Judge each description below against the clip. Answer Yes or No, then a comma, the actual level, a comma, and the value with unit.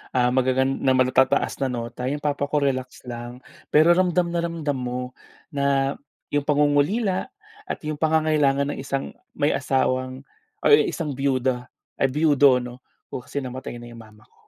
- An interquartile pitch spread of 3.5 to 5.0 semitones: No, narrow, 2.6 semitones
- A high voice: No, low, 135 Hz